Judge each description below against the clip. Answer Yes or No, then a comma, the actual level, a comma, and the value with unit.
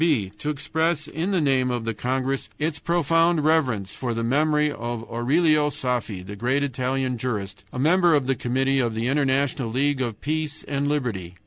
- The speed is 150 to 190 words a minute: Yes, average, 185 wpm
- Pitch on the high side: No, low, 135 Hz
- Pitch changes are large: No, average, 3.9 semitones